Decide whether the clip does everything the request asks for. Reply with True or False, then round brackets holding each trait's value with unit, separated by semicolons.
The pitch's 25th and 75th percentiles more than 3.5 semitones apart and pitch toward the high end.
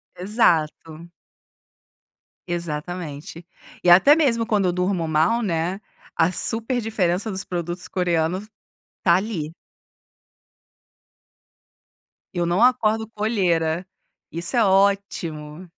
False (4.1 semitones; 180 Hz)